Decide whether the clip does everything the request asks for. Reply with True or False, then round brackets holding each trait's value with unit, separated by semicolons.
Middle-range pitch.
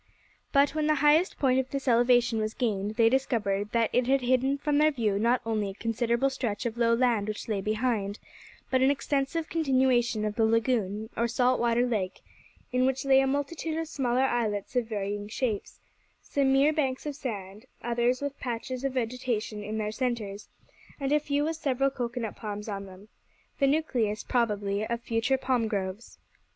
False (240 Hz)